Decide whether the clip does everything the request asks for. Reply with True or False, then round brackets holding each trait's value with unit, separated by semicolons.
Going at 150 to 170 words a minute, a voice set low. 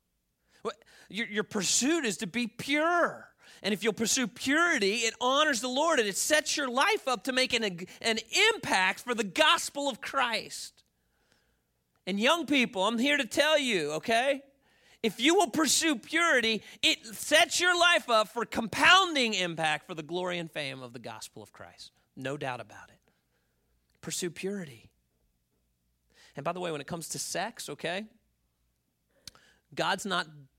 False (165 wpm; 220 Hz)